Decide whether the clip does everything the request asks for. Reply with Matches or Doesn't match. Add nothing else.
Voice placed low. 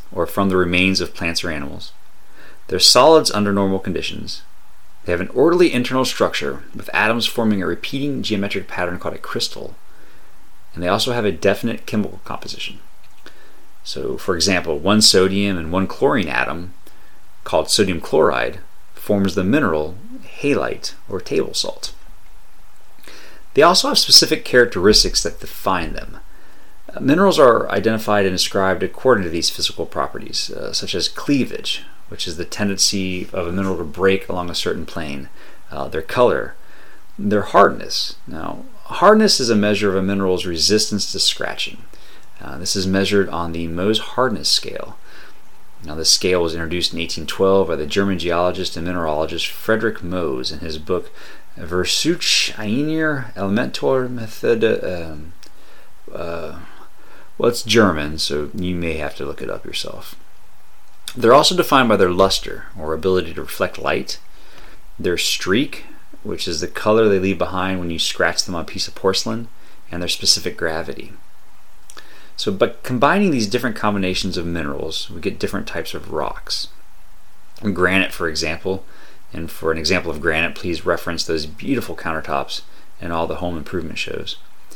Matches